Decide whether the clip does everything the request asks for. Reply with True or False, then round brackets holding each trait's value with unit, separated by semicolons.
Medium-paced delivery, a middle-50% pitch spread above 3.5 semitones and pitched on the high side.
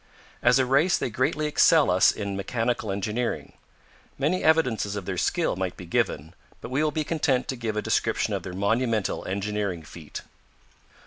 False (175 wpm; 5.5 semitones; 115 Hz)